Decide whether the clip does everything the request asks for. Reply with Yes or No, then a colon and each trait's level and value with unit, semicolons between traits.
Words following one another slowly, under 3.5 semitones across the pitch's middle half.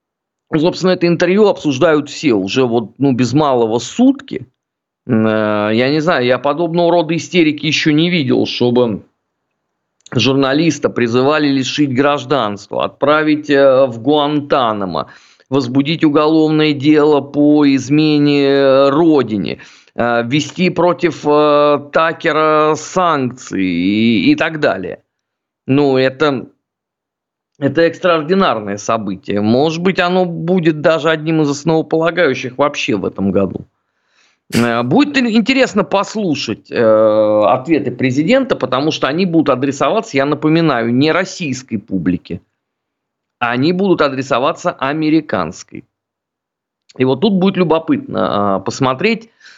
No: slow, 105 wpm; average, 4.6 semitones